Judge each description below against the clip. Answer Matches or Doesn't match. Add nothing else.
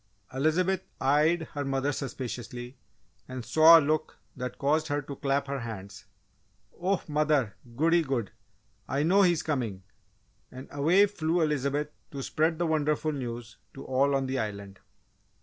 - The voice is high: Doesn't match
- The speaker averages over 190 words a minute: Doesn't match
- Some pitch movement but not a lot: Matches